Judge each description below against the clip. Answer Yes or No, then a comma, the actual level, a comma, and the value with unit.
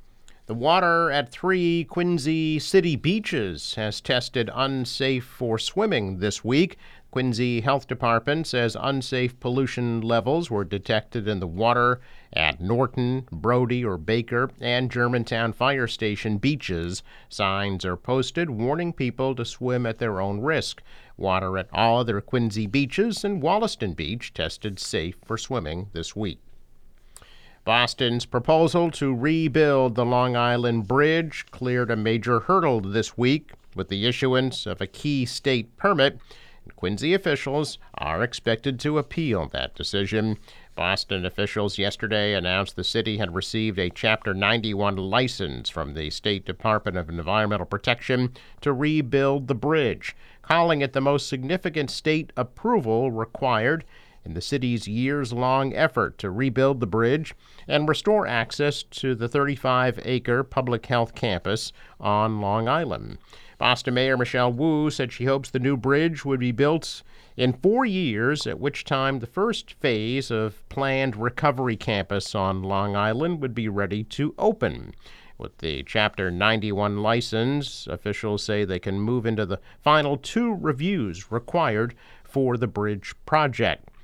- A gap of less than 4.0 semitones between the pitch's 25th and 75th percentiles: No, average, 4.5 semitones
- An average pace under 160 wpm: Yes, average, 145 wpm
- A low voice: Yes, low, 120 Hz